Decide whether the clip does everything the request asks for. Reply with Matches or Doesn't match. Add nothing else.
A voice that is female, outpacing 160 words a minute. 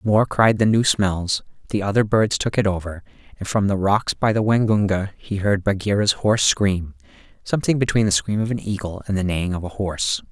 Doesn't match